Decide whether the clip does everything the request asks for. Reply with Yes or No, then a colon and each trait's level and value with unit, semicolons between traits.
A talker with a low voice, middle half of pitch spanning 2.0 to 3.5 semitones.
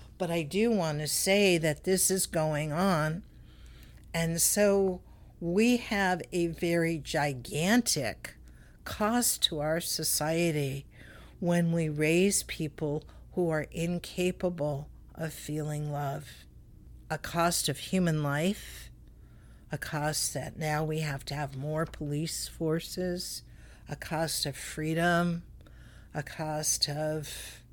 No: medium, 160 Hz; average, 2.8 semitones